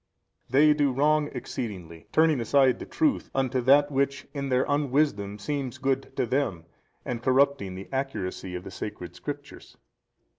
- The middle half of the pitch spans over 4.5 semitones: Yes, average, 5.0 semitones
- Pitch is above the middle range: No, low, 135 Hz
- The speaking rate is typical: Yes, average, 155 wpm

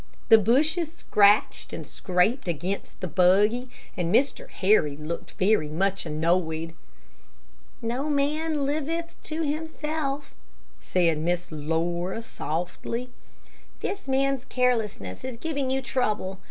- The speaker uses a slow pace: Yes, slow, 115 wpm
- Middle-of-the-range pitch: No, high, 220 Hz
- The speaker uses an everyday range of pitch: No, wide, 7.9 semitones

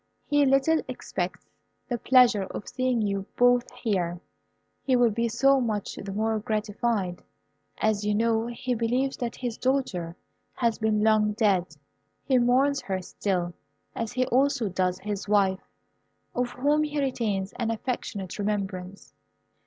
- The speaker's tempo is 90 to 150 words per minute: Yes, average, 145 wpm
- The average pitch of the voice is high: Yes, high, 225 Hz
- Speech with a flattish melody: No, average, 3.8 semitones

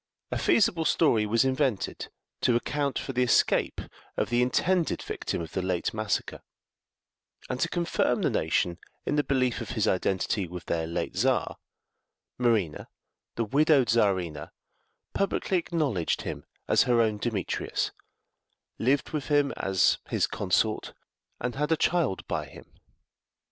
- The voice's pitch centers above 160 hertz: No, low, 120 Hz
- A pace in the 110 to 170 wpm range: Yes, average, 145 wpm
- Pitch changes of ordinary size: No, wide, 6.9 semitones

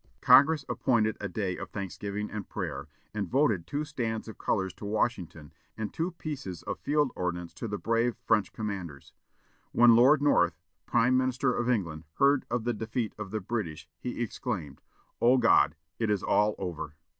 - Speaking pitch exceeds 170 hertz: No, low, 110 Hz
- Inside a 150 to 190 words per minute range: Yes, average, 170 wpm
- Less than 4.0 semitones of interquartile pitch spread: No, average, 4.8 semitones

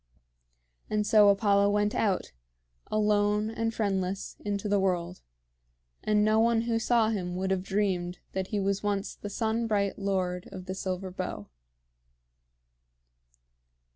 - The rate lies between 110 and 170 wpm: Yes, average, 140 wpm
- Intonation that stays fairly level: Yes, narrow, 2.0 semitones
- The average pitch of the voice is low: No, high, 200 Hz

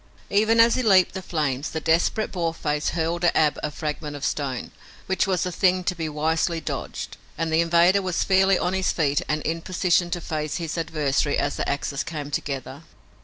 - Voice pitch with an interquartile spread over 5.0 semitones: No, average, 3.3 semitones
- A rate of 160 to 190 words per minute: No, average, 200 wpm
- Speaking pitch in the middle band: Yes, medium, 165 Hz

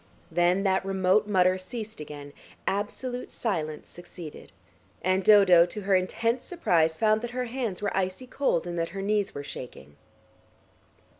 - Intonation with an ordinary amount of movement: Yes, average, 3.7 semitones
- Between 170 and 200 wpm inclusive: No, average, 150 wpm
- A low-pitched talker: No, high, 190 Hz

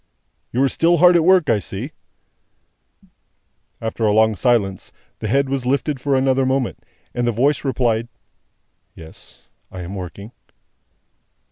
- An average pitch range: Yes, average, 4.0 semitones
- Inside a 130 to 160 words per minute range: Yes, average, 140 wpm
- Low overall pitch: Yes, low, 125 Hz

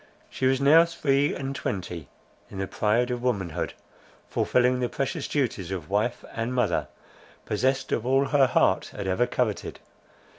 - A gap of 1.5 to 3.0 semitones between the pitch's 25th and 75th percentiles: No, average, 4.8 semitones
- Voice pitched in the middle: No, low, 125 Hz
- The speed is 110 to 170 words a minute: Yes, average, 155 wpm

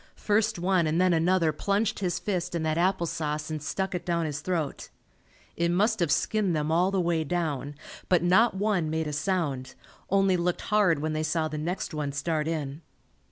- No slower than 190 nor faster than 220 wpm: Yes, average, 200 wpm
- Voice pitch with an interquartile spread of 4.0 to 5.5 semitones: No, average, 3.3 semitones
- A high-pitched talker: No, medium, 170 Hz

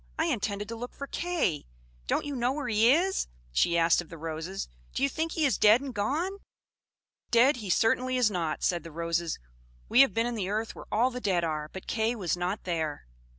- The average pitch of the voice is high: Yes, high, 220 Hz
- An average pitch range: No, wide, 6.9 semitones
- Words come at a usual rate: No, fast, 220 wpm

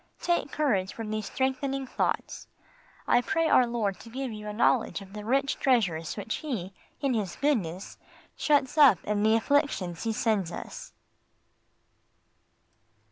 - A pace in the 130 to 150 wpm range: Yes, average, 145 wpm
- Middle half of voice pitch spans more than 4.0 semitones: Yes, average, 4.8 semitones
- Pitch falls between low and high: No, high, 225 Hz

